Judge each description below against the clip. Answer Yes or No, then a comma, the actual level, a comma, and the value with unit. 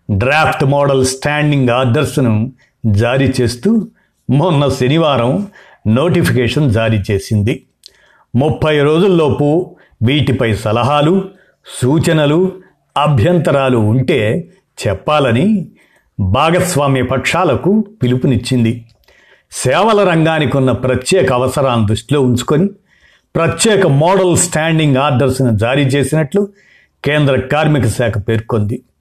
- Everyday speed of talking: Yes, average, 80 wpm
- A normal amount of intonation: Yes, average, 4.7 semitones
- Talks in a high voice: No, medium, 140 Hz